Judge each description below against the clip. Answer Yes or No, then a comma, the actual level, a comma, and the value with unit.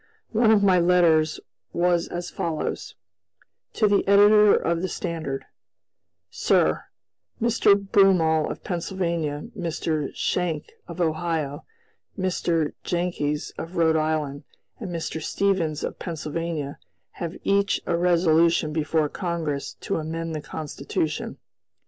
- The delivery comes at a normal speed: No, slow, 115 wpm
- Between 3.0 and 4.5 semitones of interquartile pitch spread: No, narrow, 2.5 semitones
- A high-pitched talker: No, medium, 170 Hz